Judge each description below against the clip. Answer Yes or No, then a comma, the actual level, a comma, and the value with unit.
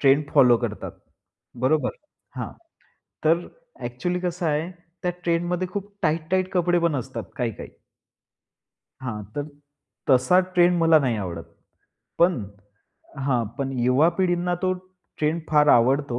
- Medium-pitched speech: Yes, medium, 155 Hz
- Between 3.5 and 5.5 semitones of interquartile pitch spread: Yes, average, 5.2 semitones